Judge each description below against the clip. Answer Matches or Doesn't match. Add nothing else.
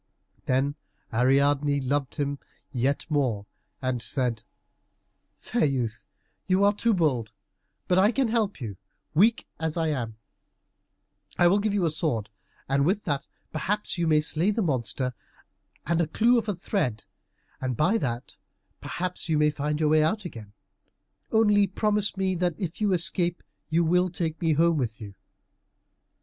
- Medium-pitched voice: Matches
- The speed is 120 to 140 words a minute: Doesn't match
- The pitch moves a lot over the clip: Matches